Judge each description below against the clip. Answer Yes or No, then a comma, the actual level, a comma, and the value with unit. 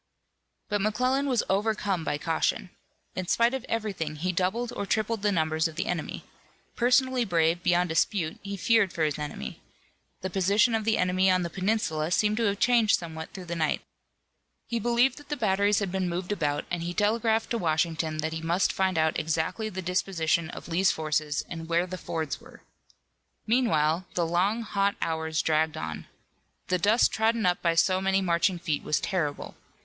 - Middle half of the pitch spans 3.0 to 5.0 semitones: Yes, average, 4.7 semitones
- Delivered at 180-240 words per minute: Yes, average, 185 wpm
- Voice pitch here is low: No, medium, 185 Hz